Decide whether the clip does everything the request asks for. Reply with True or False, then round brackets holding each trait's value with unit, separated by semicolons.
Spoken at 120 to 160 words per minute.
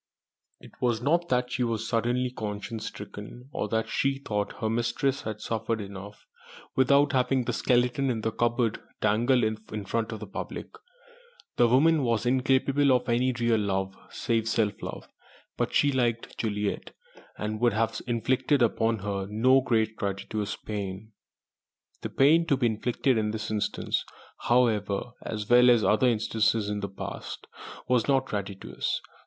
True (155 wpm)